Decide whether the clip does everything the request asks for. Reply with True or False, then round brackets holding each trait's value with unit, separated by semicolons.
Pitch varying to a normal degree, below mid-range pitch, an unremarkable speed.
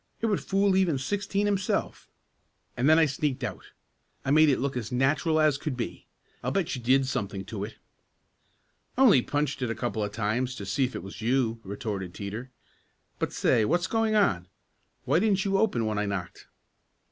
False (7.4 semitones; 130 Hz; 190 wpm)